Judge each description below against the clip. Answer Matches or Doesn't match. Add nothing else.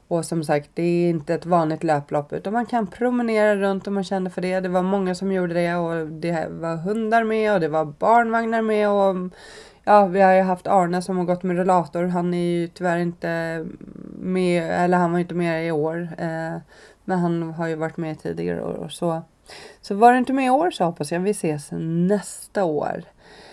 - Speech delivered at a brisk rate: Matches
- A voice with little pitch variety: Doesn't match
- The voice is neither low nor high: Matches